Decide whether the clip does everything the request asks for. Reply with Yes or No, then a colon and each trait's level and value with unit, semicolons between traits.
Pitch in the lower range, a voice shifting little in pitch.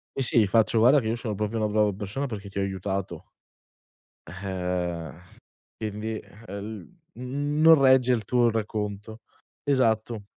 No: low, 110 Hz; average, 3.5 semitones